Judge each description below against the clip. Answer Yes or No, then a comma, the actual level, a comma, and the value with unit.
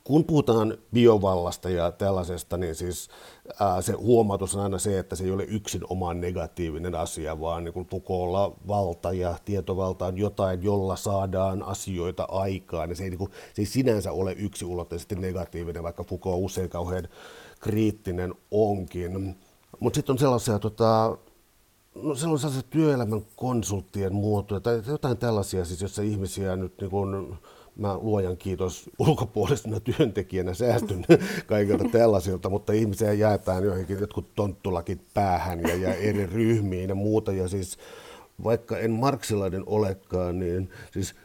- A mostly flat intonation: No, average, 3.1 semitones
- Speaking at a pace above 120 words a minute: Yes, average, 140 wpm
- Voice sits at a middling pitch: No, low, 100 Hz